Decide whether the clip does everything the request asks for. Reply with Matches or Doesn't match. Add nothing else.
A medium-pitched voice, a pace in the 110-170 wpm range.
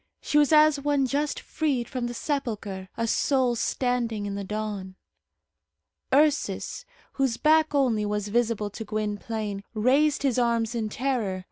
Doesn't match